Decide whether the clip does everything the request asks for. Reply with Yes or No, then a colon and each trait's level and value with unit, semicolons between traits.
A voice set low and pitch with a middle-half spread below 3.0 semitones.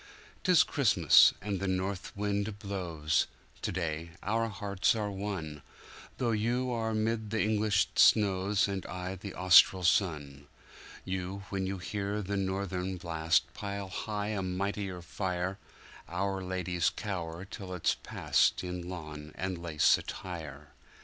Yes: very low, 95 Hz; narrow, 2.5 semitones